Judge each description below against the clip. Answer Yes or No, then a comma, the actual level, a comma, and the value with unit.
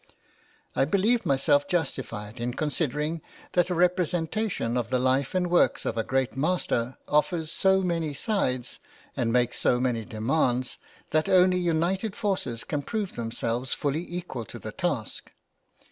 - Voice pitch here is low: No, medium, 150 Hz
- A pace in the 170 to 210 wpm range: No, average, 145 wpm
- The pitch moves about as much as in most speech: No, wide, 6.2 semitones